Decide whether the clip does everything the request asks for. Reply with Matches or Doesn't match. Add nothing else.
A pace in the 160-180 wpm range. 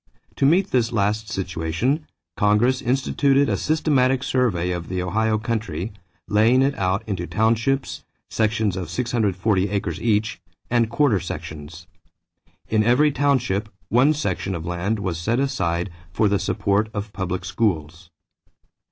Doesn't match